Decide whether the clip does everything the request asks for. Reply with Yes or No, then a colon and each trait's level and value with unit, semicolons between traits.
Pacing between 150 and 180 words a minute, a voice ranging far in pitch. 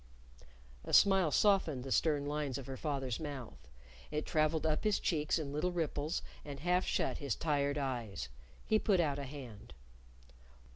No: average, 160 wpm; average, 3.0 semitones